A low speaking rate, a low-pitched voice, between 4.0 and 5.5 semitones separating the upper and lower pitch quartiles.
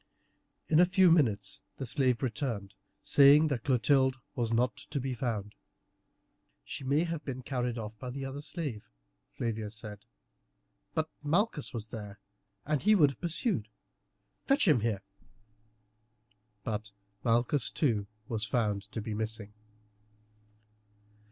Yes: slow, 130 wpm; low, 125 Hz; average, 5.0 semitones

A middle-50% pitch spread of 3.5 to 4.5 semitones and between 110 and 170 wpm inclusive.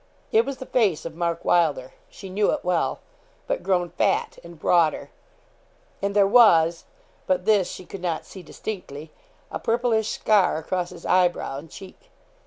Yes: average, 3.8 semitones; average, 165 wpm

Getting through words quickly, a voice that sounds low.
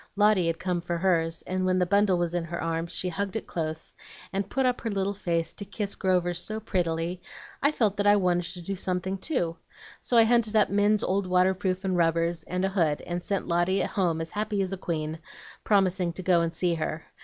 No: fast, 225 wpm; medium, 185 Hz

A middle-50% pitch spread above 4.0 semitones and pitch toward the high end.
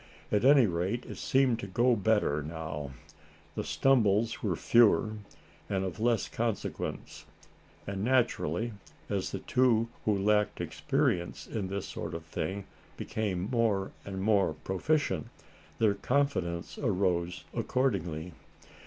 No: average, 4.5 semitones; low, 100 Hz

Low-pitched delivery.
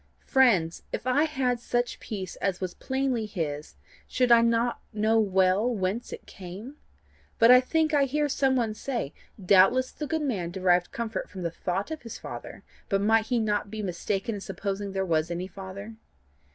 No: high, 215 Hz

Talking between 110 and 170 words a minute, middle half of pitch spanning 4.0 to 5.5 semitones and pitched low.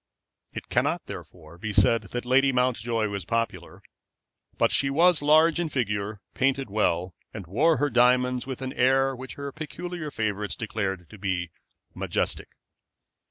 Yes: average, 155 wpm; average, 4.9 semitones; low, 125 Hz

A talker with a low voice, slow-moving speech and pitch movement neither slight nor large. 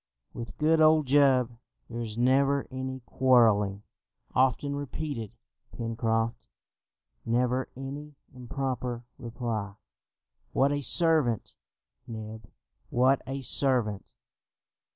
Yes: low, 125 Hz; slow, 90 wpm; average, 3.1 semitones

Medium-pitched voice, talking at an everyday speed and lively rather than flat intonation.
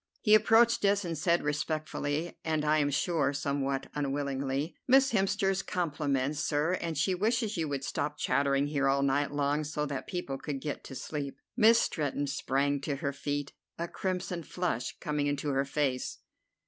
No: medium, 145 Hz; average, 170 wpm; average, 3.6 semitones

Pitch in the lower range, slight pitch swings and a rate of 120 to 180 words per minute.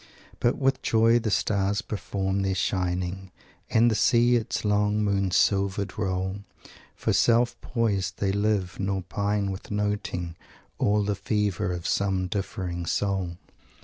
Yes: low, 100 Hz; narrow, 1.8 semitones; average, 140 wpm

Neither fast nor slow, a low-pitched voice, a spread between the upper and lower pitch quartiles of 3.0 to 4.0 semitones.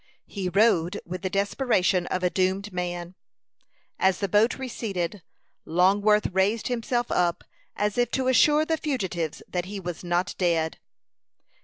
No: average, 145 wpm; high, 190 Hz; average, 3.7 semitones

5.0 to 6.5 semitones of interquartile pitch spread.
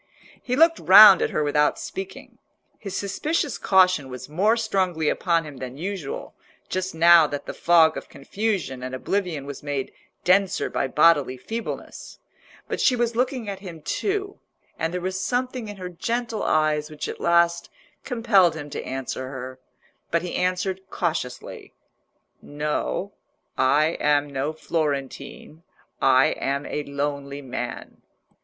Yes: wide, 5.5 semitones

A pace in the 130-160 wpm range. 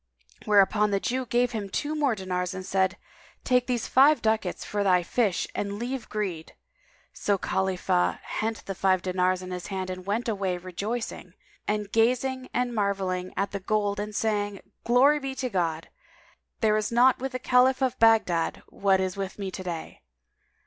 No: average, 170 wpm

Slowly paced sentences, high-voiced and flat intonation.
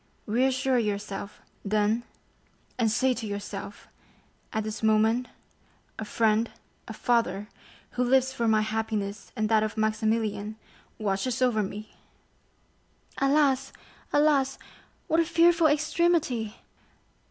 No: slow, 110 wpm; high, 225 Hz; average, 3.6 semitones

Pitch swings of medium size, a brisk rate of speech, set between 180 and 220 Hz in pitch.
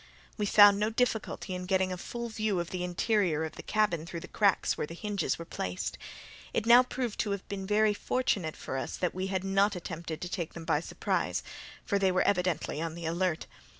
Yes: average, 3.5 semitones; fast, 220 wpm; high, 190 Hz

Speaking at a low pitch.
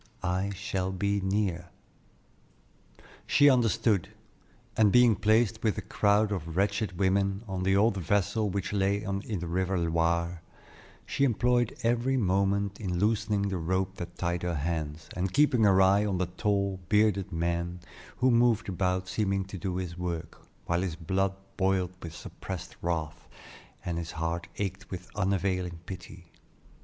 Yes: very low, 95 Hz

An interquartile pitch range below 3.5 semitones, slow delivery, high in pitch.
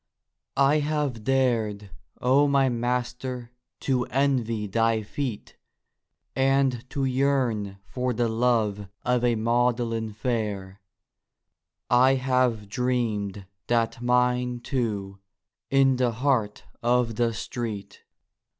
No: narrow, 2.6 semitones; slow, 105 wpm; low, 120 Hz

